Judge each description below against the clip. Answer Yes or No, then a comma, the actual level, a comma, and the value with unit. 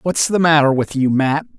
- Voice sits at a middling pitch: Yes, medium, 150 Hz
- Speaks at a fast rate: Yes, fast, 225 wpm